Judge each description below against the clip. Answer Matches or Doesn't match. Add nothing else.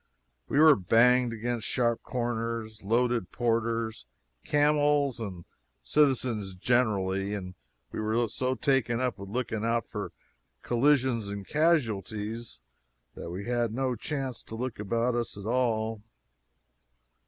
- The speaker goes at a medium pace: Doesn't match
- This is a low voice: Matches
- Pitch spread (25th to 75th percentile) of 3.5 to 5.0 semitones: Doesn't match